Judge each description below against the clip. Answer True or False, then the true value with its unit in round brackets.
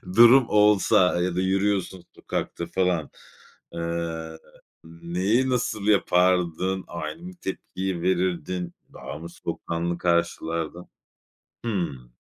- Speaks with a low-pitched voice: True (90 Hz)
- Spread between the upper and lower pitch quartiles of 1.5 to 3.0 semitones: True (2.5 semitones)